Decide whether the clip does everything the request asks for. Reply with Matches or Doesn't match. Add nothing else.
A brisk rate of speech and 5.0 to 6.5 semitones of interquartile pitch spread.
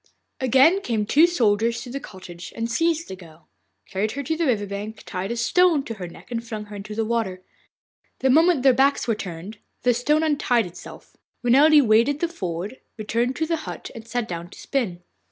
Matches